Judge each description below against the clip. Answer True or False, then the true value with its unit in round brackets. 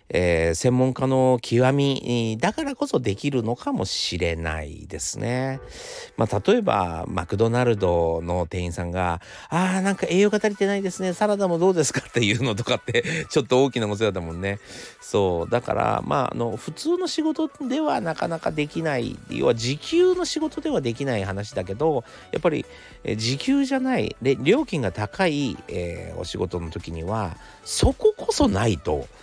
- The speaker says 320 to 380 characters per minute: True (335 characters per minute)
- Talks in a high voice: False (125 Hz)